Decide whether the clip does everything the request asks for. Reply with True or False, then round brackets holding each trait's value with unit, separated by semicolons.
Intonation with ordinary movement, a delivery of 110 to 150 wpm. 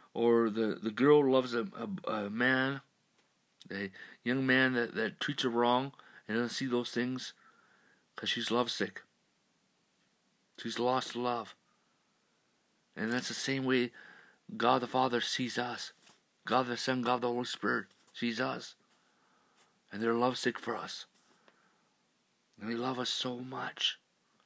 False (1.7 semitones; 140 wpm)